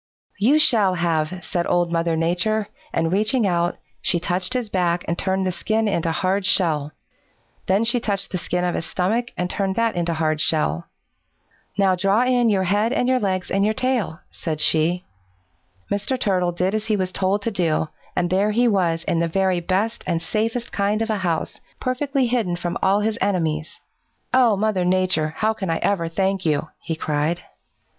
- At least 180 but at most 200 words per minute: Yes, average, 190 wpm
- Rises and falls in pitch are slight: No, average, 4.0 semitones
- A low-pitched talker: No, medium, 185 Hz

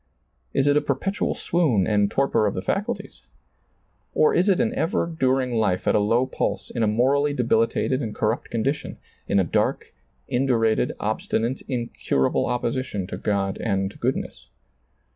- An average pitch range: Yes, average, 4.6 semitones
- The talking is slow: No, average, 155 wpm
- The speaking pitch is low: Yes, low, 120 Hz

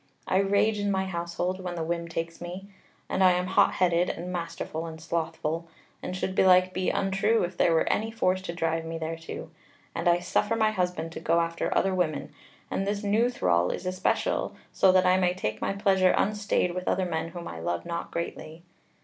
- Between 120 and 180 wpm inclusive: No, fast, 205 wpm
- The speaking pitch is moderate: Yes, medium, 180 Hz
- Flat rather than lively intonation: Yes, narrow, 2.3 semitones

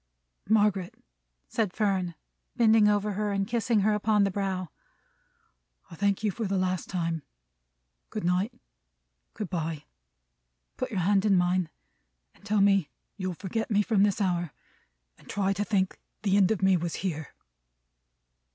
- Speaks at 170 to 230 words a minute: No, average, 150 wpm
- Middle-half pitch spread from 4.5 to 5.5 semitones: No, narrow, 2.4 semitones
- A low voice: No, high, 195 Hz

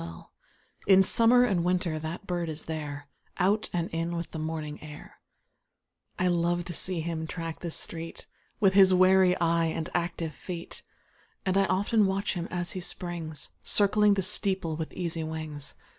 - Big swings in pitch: No, average, 2.8 semitones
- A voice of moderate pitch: Yes, medium, 175 Hz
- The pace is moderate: Yes, average, 180 wpm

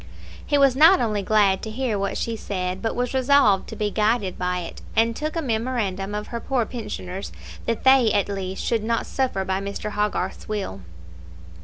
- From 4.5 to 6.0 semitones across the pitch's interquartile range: No, average, 3.9 semitones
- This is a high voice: Yes, high, 215 Hz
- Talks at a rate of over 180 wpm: Yes, average, 190 wpm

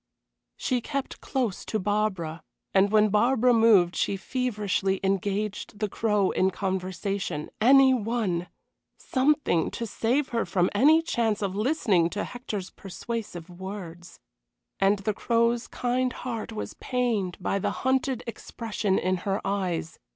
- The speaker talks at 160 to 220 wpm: No, slow, 135 wpm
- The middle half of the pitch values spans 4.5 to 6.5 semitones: No, average, 3.9 semitones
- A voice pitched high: Yes, high, 210 Hz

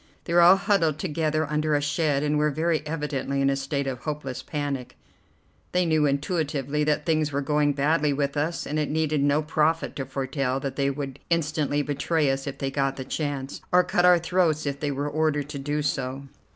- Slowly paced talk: No, fast, 205 wpm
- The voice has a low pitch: No, medium, 145 Hz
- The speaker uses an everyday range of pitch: No, narrow, 2.0 semitones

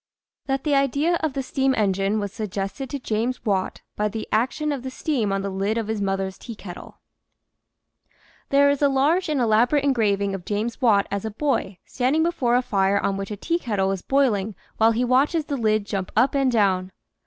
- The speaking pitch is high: Yes, high, 225 Hz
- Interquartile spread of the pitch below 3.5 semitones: No, wide, 5.4 semitones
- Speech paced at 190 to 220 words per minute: Yes, average, 200 wpm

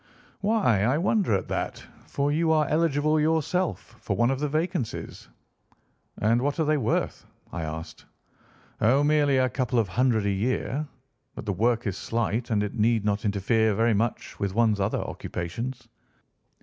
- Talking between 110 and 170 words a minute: Yes, average, 165 wpm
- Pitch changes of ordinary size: No, wide, 5.7 semitones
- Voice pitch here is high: No, low, 120 Hz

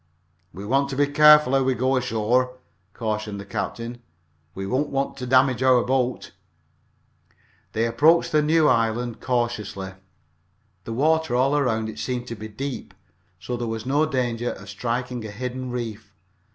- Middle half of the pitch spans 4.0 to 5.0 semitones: No, average, 3.0 semitones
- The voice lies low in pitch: Yes, low, 125 Hz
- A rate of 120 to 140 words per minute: No, average, 160 wpm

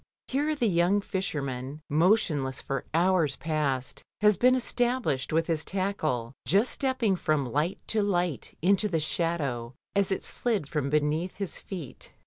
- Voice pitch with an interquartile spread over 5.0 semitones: Yes, wide, 5.6 semitones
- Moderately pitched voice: Yes, medium, 170 Hz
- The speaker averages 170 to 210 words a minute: No, average, 150 wpm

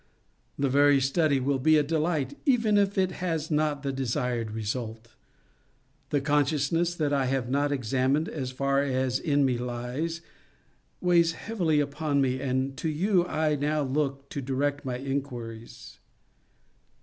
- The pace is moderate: Yes, average, 150 wpm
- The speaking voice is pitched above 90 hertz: Yes, medium, 140 Hz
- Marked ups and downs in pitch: No, average, 3.0 semitones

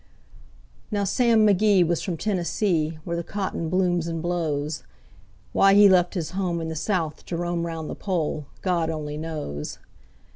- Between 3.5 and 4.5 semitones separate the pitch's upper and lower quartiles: No, average, 3.0 semitones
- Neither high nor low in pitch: Yes, medium, 170 Hz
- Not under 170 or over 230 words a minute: No, average, 160 wpm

